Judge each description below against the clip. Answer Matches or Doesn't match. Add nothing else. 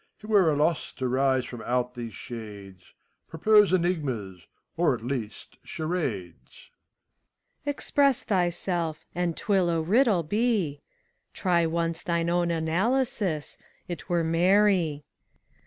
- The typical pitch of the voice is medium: Matches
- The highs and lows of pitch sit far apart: Matches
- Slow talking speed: Matches